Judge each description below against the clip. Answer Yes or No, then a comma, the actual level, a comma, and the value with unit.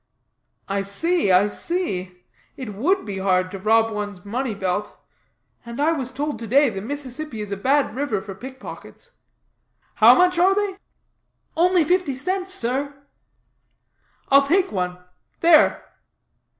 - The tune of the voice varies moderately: No, wide, 8.2 semitones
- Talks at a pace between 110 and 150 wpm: Yes, average, 145 wpm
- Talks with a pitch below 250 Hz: No, very high, 260 Hz